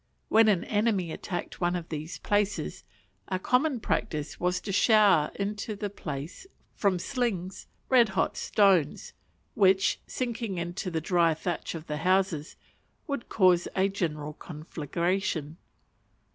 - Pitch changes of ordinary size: Yes, average, 3.9 semitones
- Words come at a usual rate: No, slow, 130 wpm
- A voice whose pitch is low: No, medium, 185 Hz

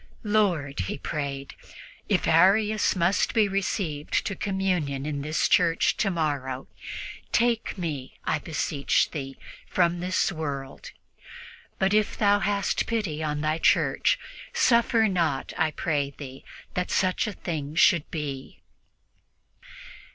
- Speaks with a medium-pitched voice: Yes, medium, 165 Hz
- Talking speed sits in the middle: No, slow, 120 wpm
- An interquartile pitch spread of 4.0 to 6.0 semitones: Yes, wide, 5.4 semitones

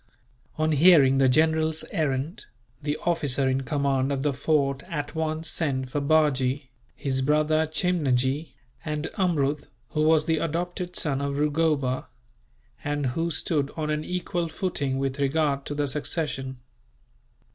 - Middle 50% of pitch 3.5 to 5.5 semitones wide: No, average, 2.7 semitones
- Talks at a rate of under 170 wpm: Yes, average, 140 wpm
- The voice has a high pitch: No, medium, 150 Hz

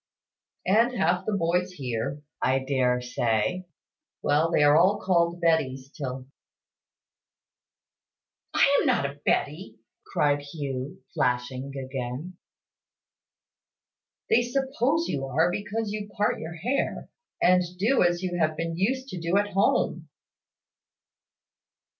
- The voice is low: No, medium, 165 Hz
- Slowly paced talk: Yes, slow, 120 wpm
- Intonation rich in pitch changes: Yes, wide, 6.4 semitones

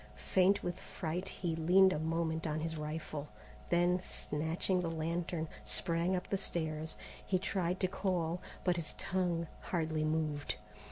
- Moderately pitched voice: Yes, medium, 170 Hz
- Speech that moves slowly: No, average, 150 wpm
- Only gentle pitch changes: Yes, narrow, 2.3 semitones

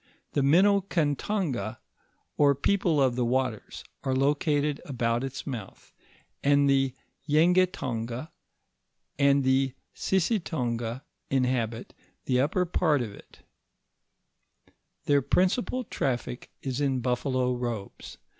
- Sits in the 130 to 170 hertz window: Yes, low, 135 Hz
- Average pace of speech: No, slow, 110 wpm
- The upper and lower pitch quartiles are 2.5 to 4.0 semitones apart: Yes, average, 3.5 semitones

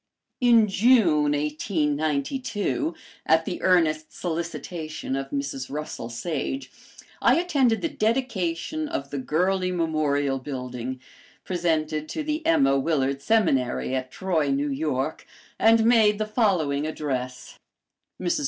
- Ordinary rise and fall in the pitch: No, wide, 7.0 semitones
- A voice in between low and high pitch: Yes, medium, 160 Hz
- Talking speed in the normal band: No, slow, 115 wpm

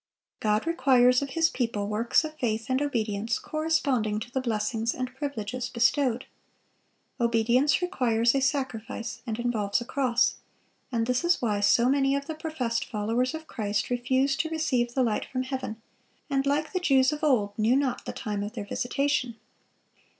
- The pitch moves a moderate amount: Yes, average, 3.6 semitones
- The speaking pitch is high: Yes, very high, 250 Hz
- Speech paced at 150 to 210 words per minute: Yes, average, 170 wpm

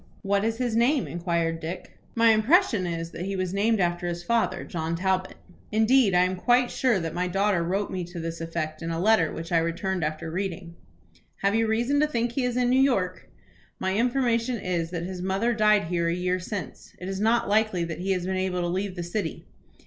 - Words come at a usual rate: No, fast, 220 wpm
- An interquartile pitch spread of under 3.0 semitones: No, average, 4.5 semitones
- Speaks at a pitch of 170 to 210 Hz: Yes, high, 190 Hz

